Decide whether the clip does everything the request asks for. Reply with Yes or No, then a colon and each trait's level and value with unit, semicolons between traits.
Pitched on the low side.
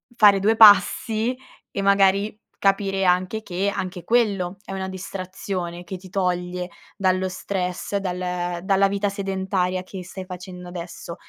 No: high, 190 Hz